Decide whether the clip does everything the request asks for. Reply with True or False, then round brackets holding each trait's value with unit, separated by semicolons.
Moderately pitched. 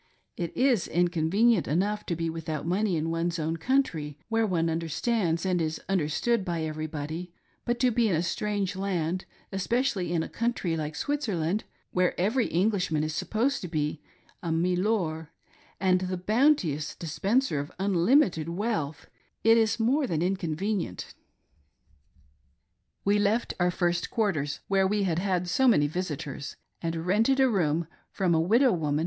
True (180 Hz)